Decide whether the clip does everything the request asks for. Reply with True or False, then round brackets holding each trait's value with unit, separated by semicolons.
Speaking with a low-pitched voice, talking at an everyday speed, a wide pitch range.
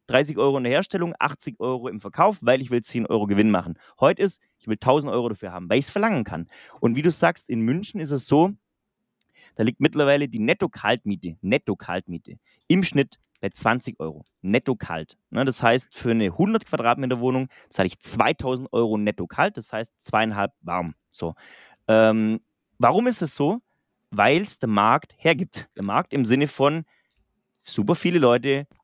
True (130 Hz; 180 wpm; 6.0 semitones)